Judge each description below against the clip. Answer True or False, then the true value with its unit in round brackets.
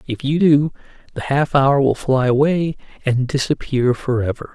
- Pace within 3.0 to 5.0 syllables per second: True (4.4 syllables/s)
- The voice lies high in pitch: False (135 Hz)